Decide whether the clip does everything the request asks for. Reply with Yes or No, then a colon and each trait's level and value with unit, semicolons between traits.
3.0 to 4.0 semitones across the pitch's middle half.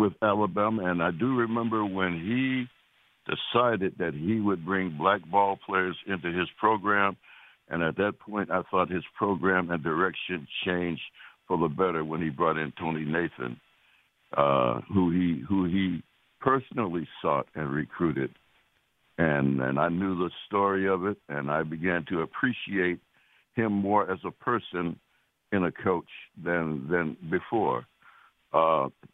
Yes: average, 3.5 semitones